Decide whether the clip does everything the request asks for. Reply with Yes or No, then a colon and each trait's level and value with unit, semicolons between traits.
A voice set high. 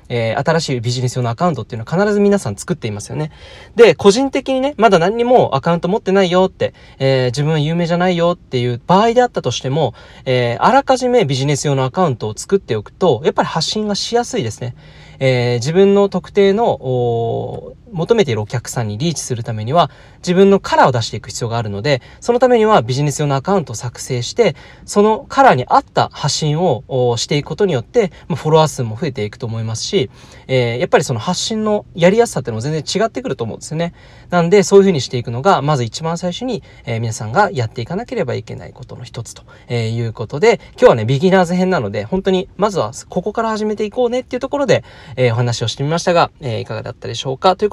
No: medium, 150 Hz